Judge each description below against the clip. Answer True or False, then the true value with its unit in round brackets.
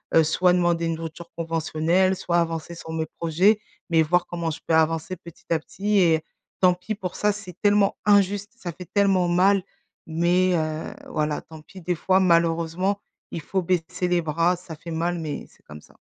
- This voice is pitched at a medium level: True (170 Hz)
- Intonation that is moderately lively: False (2.3 semitones)